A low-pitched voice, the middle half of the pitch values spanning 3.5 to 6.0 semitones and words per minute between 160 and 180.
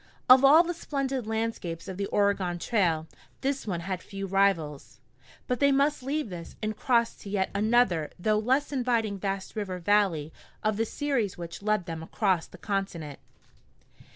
No: high, 205 Hz; average, 5.3 semitones; average, 165 wpm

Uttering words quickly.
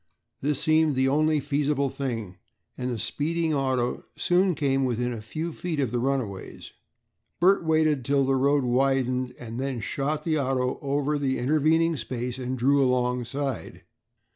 No: average, 155 wpm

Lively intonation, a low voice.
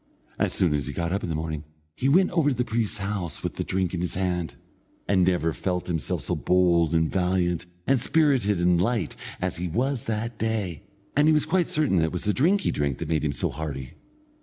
Yes: wide, 5.9 semitones; very low, 90 Hz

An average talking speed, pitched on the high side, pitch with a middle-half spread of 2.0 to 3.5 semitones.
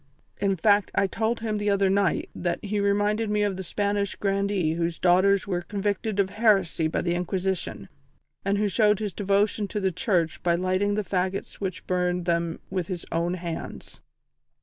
Yes: average, 180 wpm; high, 195 Hz; narrow, 2.4 semitones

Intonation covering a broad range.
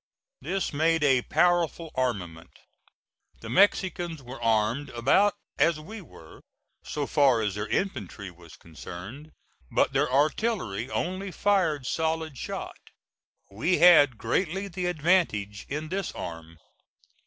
Yes: wide, 7.9 semitones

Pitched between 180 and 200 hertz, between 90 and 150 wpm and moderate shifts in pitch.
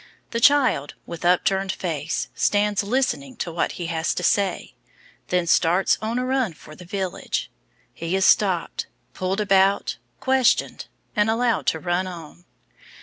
Yes: high, 190 Hz; average, 145 wpm; average, 4.2 semitones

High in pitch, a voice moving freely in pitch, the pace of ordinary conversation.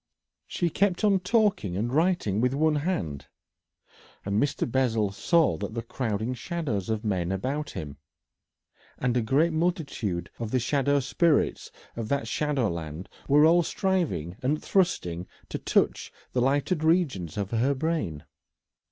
No: low, 130 Hz; wide, 7.9 semitones; average, 145 wpm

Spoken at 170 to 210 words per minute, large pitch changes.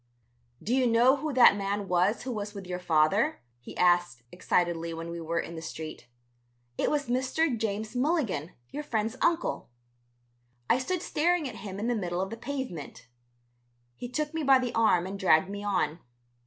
Yes: average, 180 wpm; wide, 6.7 semitones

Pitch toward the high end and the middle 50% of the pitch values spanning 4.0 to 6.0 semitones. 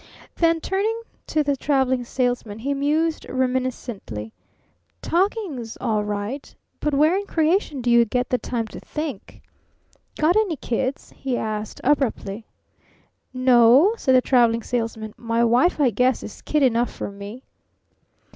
Yes: very high, 255 Hz; average, 4.7 semitones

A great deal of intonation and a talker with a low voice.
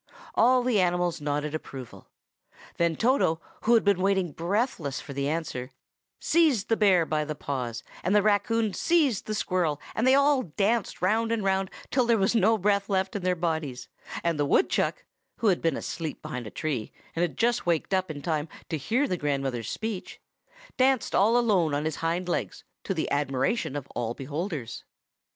No: wide, 6.6 semitones; medium, 180 Hz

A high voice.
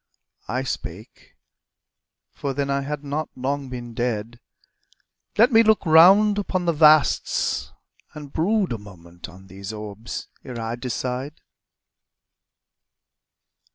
No: low, 135 Hz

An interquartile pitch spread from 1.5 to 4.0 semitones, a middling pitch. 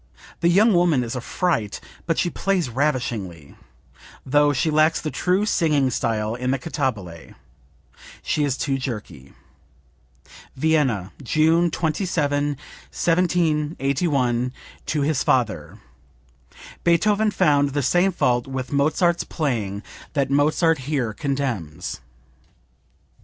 No: average, 4.8 semitones; medium, 145 Hz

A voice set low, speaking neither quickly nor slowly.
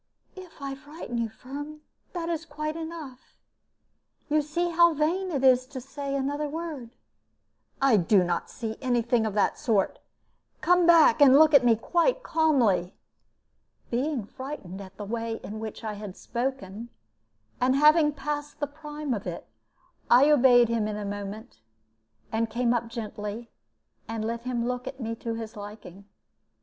No: very high, 255 Hz; average, 165 wpm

